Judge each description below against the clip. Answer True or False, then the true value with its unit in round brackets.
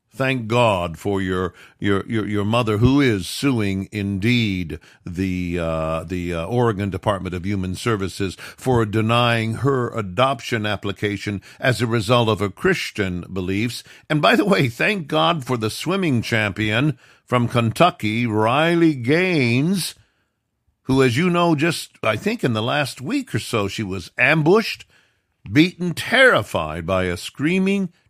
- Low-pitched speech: True (115 Hz)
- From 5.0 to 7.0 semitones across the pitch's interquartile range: True (5.3 semitones)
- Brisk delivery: False (145 wpm)